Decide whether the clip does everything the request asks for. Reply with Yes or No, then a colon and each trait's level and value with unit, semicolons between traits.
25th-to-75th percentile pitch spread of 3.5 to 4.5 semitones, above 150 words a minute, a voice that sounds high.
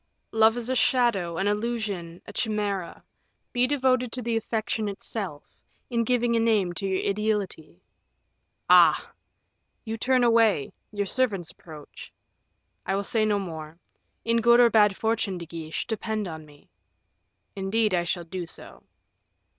No: average, 4.0 semitones; average, 145 wpm; high, 210 Hz